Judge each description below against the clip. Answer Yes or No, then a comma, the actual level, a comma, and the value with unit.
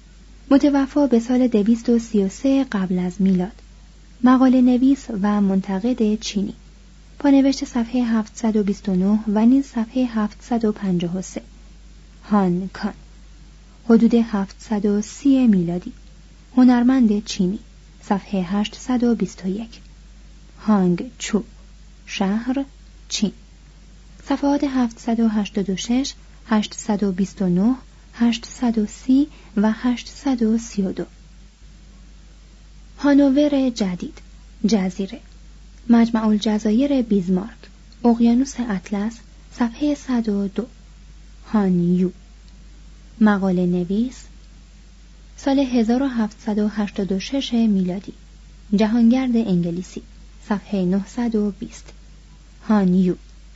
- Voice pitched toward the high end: Yes, high, 215 Hz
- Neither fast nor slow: No, slow, 70 wpm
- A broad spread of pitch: No, average, 3.8 semitones